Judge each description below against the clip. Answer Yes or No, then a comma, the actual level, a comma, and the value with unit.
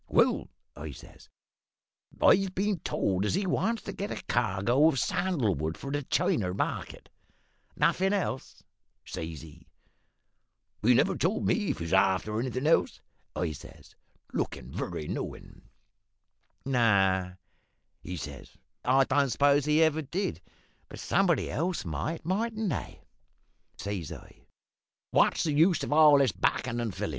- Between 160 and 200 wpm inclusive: No, average, 145 wpm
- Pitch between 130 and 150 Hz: Yes, low, 135 Hz